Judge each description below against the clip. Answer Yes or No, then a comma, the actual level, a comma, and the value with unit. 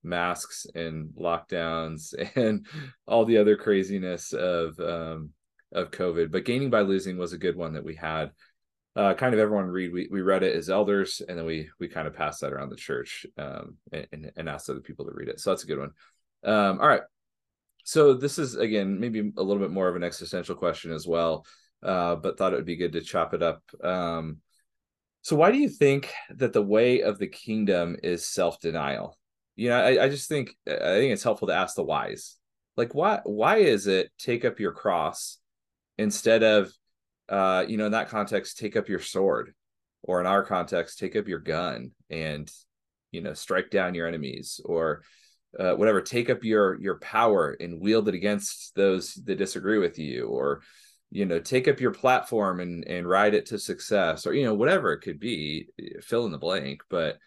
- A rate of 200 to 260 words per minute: Yes, fast, 205 wpm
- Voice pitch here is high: No, very low, 95 Hz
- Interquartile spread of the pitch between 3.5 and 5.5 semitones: Yes, average, 4.2 semitones